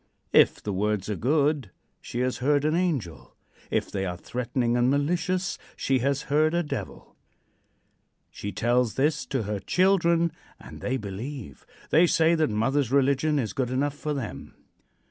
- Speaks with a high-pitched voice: No, low, 135 Hz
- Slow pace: No, average, 160 wpm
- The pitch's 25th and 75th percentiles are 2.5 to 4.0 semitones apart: No, average, 4.6 semitones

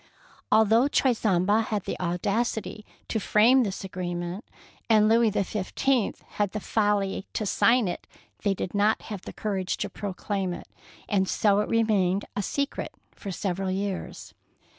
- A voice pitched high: Yes, high, 205 Hz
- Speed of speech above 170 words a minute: No, average, 145 wpm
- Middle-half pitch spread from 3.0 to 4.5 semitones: No, narrow, 2.6 semitones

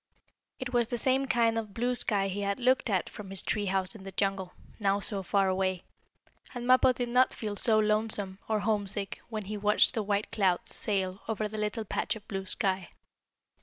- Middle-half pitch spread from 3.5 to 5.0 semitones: No, narrow, 2.6 semitones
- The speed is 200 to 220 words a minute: Yes, fast, 205 wpm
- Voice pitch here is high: Yes, high, 210 Hz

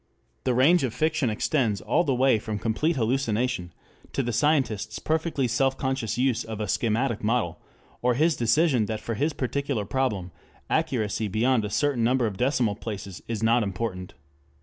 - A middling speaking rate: Yes, average, 170 wpm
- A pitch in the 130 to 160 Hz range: No, low, 120 Hz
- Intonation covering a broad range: No, average, 3.8 semitones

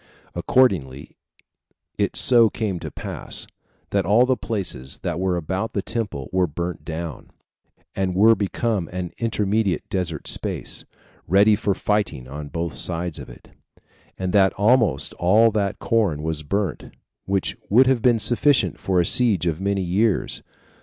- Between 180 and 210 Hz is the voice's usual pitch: No, very low, 95 Hz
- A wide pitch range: No, average, 4.2 semitones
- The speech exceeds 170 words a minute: No, average, 150 wpm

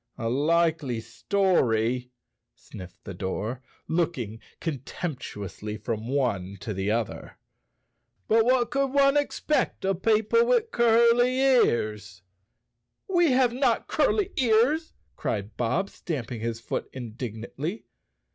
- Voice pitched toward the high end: No, medium, 150 Hz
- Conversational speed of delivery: No, slow, 120 wpm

